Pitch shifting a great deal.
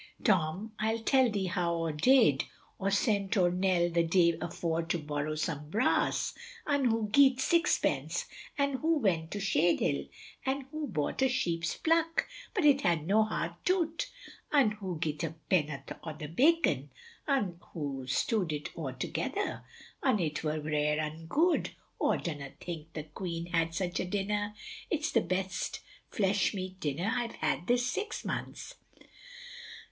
Yes: wide, 6.8 semitones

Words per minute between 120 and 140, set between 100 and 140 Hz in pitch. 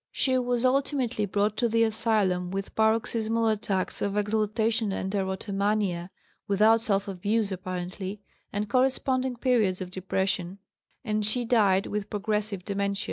No: slow, 135 wpm; high, 210 Hz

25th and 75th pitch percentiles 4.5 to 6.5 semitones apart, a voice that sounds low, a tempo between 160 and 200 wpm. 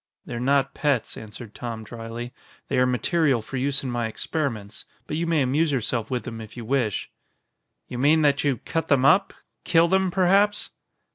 Yes: average, 4.9 semitones; low, 130 Hz; average, 185 wpm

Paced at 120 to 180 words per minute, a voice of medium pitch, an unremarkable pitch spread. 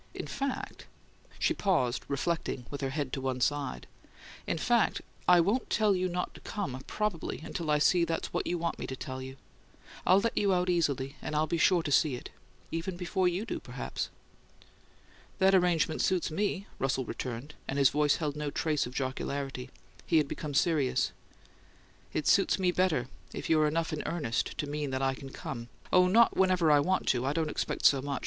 No: average, 200 wpm; medium, 155 Hz; average, 4.8 semitones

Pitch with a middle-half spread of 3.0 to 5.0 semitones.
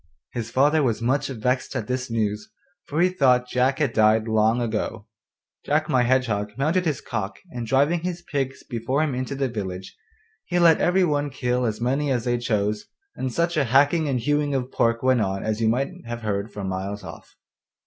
Yes: average, 4.4 semitones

